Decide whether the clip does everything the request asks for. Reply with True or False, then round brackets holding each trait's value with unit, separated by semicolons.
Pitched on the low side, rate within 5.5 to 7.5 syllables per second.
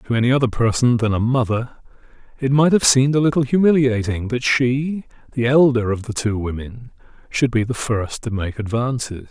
False (120 Hz; 5.3 syllables/s)